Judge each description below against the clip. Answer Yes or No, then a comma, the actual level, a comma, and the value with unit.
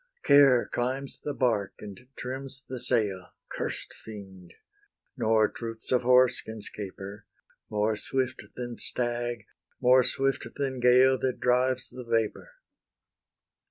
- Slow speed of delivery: Yes, slow, 125 wpm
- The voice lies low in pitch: Yes, low, 125 Hz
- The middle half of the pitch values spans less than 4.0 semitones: Yes, average, 2.8 semitones